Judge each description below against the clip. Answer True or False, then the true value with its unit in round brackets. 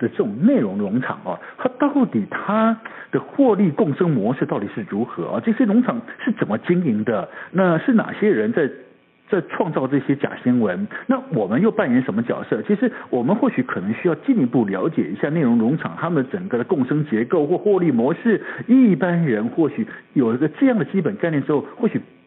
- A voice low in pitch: False (220 Hz)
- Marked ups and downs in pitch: False (4.8 semitones)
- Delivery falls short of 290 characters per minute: False (300 characters per minute)